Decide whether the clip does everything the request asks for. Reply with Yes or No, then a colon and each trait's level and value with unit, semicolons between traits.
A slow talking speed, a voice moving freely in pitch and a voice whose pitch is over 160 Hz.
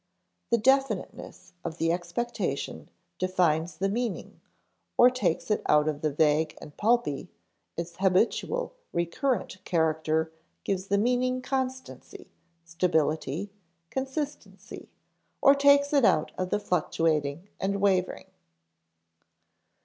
Yes: slow, 110 wpm; wide, 7.3 semitones; medium, 185 Hz